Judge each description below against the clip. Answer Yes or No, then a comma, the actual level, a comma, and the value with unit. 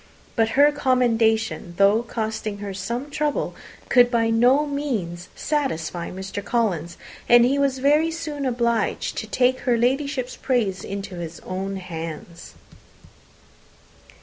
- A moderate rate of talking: No, slow, 125 wpm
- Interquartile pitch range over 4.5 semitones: Yes, average, 5.3 semitones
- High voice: Yes, high, 235 Hz